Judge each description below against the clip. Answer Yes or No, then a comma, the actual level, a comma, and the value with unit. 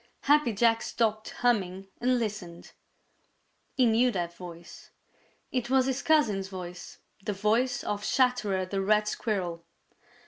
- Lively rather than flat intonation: No, average, 4.6 semitones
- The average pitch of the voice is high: Yes, high, 210 Hz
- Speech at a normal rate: No, slow, 130 wpm